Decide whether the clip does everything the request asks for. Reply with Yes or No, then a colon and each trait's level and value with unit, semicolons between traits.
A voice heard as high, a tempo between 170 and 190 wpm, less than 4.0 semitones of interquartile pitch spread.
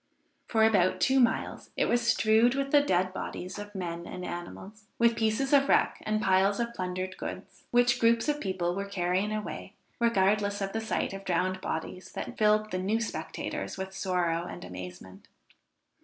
Yes: high, 200 Hz; average, 175 wpm; average, 3.6 semitones